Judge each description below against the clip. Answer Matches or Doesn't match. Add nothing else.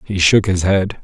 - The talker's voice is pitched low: Matches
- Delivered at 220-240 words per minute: Matches